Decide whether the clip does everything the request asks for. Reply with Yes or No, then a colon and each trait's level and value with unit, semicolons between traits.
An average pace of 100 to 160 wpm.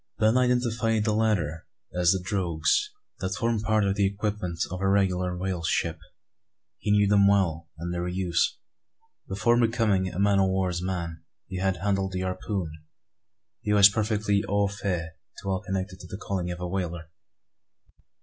No: average, 170 wpm